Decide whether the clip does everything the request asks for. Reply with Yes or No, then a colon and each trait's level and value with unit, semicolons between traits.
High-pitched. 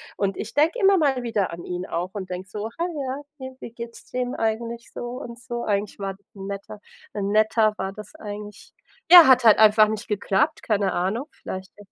Yes: high, 215 Hz